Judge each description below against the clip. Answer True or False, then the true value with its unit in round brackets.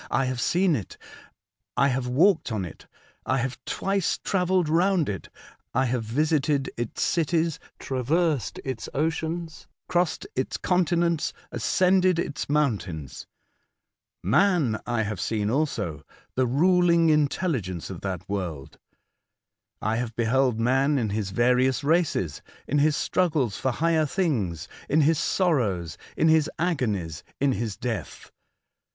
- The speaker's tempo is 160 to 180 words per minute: False (135 wpm)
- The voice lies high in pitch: False (135 Hz)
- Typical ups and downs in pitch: False (6.7 semitones)